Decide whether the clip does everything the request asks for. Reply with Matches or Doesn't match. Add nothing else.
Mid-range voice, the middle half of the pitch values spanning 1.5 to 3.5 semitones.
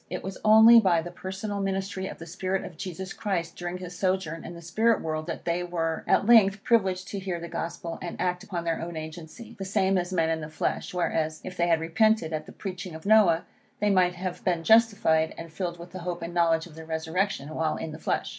Matches